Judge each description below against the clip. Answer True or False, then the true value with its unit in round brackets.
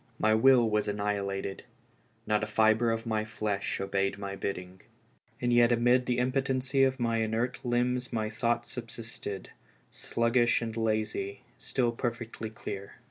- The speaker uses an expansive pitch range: False (2.4 semitones)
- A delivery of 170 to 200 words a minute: False (145 wpm)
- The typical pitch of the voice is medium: False (115 Hz)